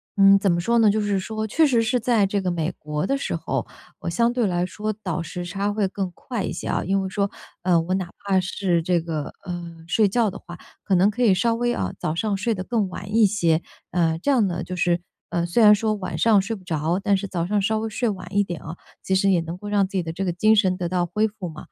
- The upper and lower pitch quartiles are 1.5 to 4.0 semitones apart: Yes, average, 3.5 semitones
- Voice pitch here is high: Yes, high, 195 Hz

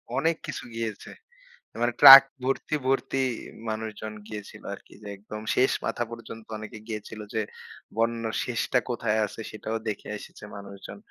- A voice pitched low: Yes, low, 110 Hz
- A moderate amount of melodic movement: No, narrow, 2.0 semitones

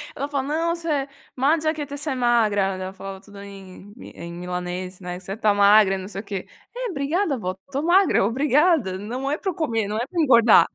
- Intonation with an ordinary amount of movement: No, wide, 7.4 semitones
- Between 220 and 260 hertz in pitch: Yes, high, 230 Hz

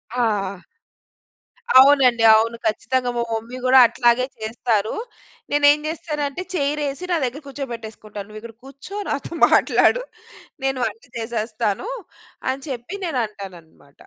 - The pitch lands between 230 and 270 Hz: Yes, high, 240 Hz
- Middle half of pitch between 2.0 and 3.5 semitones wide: No, average, 4.2 semitones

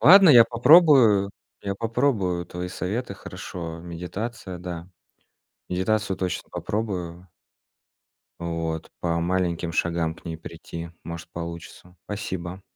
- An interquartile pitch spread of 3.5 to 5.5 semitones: Yes, average, 3.8 semitones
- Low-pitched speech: Yes, very low, 90 Hz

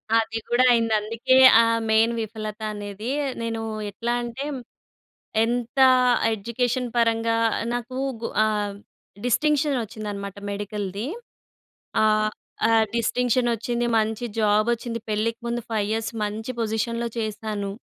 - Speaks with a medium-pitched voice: No, high, 225 Hz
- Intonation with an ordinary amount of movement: No, narrow, 1.8 semitones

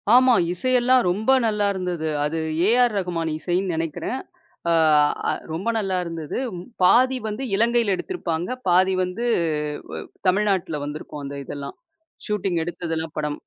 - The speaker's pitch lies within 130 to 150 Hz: No, medium, 185 Hz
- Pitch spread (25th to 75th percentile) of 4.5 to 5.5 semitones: Yes, average, 5.0 semitones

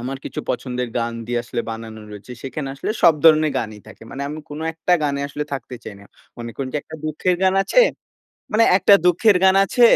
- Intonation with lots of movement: Yes, wide, 5.9 semitones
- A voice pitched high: No, medium, 140 Hz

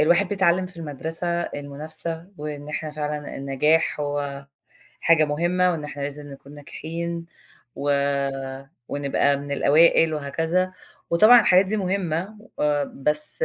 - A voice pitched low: No, medium, 155 Hz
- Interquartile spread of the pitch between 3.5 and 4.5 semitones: No, average, 3.0 semitones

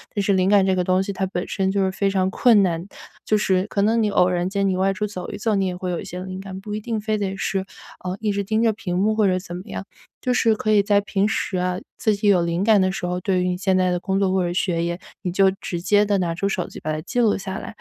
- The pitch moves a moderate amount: No, narrow, 2.0 semitones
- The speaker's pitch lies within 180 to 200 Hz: Yes, high, 195 Hz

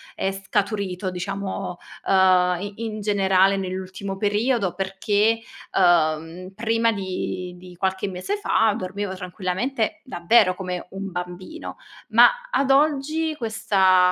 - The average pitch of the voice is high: Yes, high, 195 Hz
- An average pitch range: Yes, average, 3.2 semitones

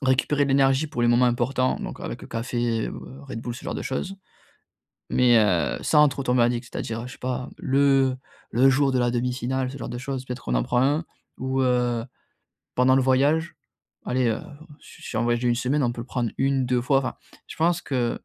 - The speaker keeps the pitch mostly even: Yes, narrow, 2.0 semitones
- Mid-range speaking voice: No, low, 125 Hz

